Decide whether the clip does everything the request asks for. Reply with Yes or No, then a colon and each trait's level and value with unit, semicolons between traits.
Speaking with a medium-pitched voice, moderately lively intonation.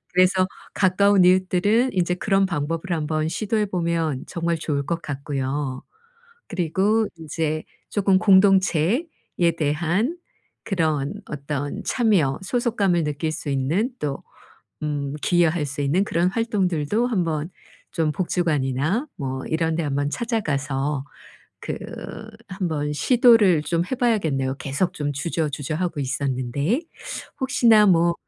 Yes: medium, 165 Hz; average, 4.9 semitones